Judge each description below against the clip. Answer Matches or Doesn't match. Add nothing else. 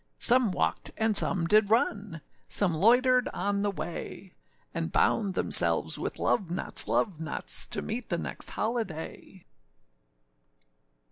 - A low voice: Doesn't match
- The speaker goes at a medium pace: Doesn't match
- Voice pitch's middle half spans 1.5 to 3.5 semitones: Doesn't match